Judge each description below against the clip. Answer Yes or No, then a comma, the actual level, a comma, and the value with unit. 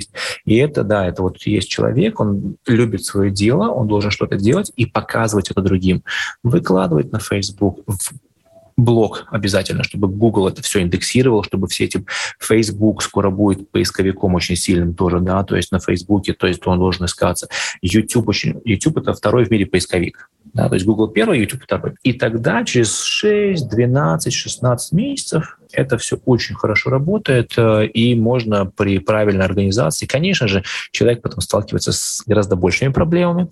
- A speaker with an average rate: No, fast, 165 wpm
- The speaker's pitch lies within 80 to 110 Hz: Yes, low, 105 Hz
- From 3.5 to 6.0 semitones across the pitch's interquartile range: Yes, average, 3.8 semitones